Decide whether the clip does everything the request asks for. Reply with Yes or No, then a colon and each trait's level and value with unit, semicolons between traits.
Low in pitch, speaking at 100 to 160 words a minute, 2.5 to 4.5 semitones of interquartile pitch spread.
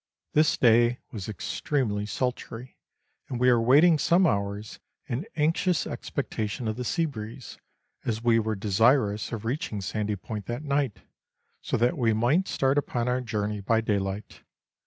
Yes: low, 115 Hz; average, 155 wpm; average, 4.1 semitones